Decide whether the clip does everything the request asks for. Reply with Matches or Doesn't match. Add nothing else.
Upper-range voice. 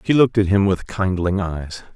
Doesn't match